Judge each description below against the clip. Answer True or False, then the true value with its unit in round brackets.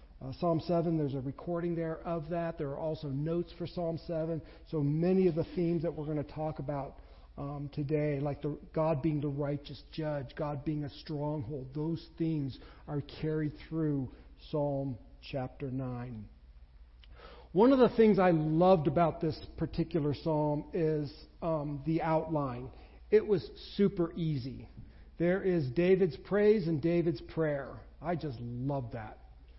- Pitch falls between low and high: True (155 Hz)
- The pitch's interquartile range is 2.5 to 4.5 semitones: True (3.3 semitones)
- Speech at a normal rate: True (155 wpm)